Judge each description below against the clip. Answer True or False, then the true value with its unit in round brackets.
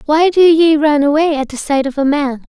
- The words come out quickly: True (265 wpm)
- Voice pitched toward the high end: True (295 Hz)